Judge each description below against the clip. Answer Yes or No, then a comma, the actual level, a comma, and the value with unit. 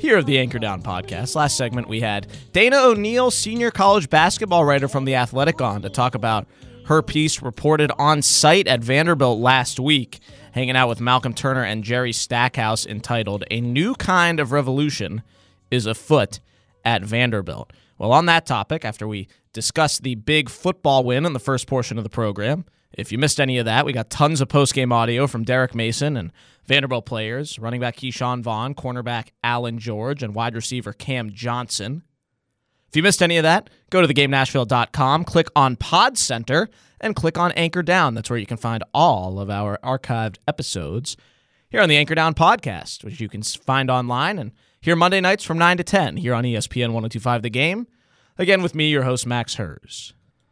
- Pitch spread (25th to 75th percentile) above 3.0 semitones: Yes, average, 4.6 semitones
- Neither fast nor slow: Yes, average, 190 wpm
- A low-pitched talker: Yes, low, 130 Hz